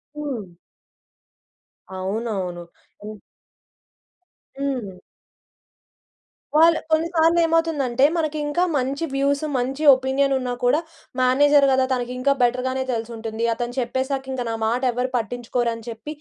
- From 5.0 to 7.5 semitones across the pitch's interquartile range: No, average, 3.3 semitones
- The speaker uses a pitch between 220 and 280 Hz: Yes, very high, 255 Hz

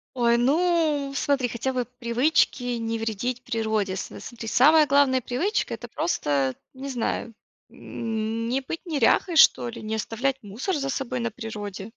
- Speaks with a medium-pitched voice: No, high, 245 Hz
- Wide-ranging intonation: No, average, 3.7 semitones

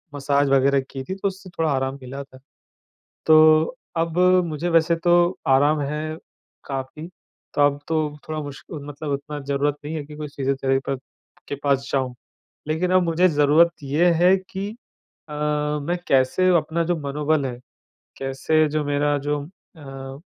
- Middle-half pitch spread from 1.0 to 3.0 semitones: Yes, narrow, 2.6 semitones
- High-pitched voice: No, medium, 150 Hz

